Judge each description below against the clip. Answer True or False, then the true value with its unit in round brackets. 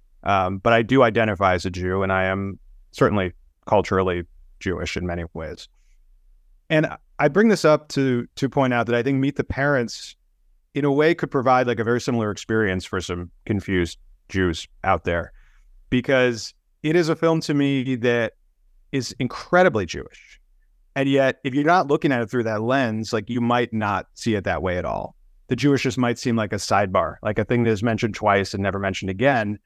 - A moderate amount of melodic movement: False (6.2 semitones)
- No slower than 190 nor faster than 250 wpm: True (200 wpm)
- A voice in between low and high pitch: False (110 Hz)